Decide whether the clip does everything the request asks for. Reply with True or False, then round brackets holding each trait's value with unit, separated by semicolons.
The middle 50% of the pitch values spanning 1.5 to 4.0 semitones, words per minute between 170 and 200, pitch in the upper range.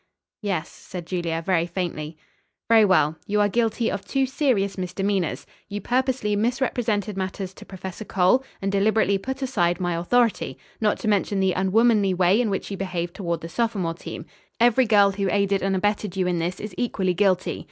True (3.1 semitones; 180 wpm; 195 Hz)